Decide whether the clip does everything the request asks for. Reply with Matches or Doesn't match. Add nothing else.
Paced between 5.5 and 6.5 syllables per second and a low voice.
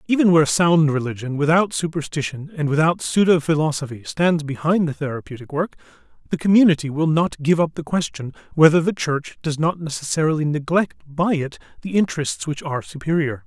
Doesn't match